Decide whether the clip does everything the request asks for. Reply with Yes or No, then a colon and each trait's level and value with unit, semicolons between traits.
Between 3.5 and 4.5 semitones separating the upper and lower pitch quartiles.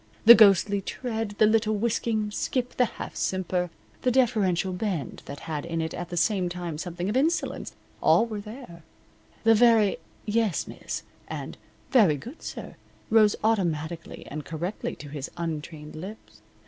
No: average, 4.9 semitones